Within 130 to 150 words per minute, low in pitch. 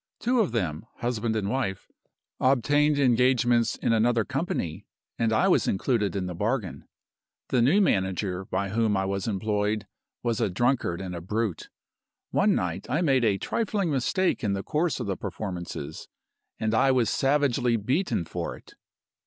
No: average, 160 wpm; low, 115 Hz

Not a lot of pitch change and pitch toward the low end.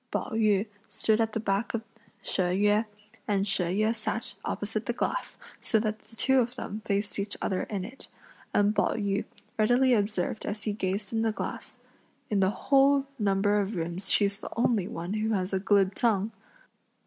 No: narrow, 2.1 semitones; high, 210 Hz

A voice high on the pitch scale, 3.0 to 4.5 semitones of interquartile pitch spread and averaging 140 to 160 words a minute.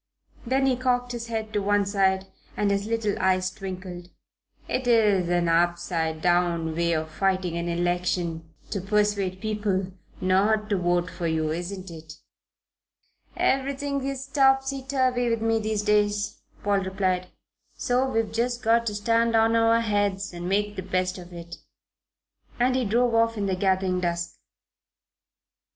Yes: high, 200 Hz; average, 4.2 semitones; average, 150 wpm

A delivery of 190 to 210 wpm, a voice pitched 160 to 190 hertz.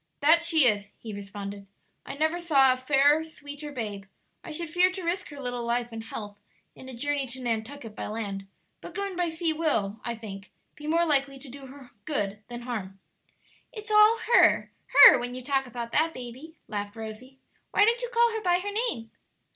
No: average, 200 wpm; very high, 270 Hz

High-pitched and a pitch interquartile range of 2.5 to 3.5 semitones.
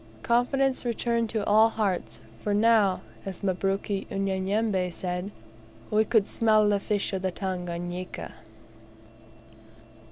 Yes: high, 200 Hz; average, 2.9 semitones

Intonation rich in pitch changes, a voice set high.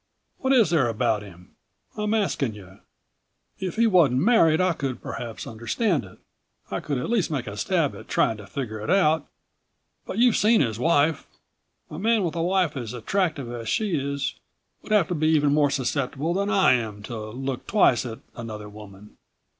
No: wide, 8.1 semitones; medium, 140 Hz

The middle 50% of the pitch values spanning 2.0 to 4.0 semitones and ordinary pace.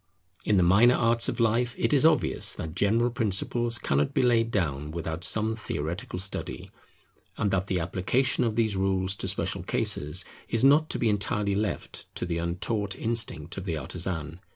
No: average, 4.8 semitones; average, 175 wpm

